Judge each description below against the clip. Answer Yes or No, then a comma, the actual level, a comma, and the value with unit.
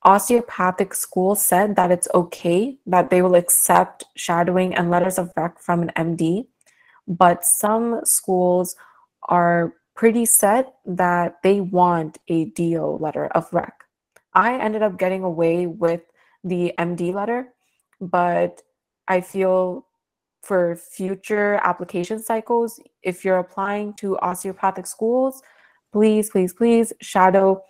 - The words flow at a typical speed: No, slow, 125 wpm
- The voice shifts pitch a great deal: No, average, 3.0 semitones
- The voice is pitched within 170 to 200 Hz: Yes, medium, 185 Hz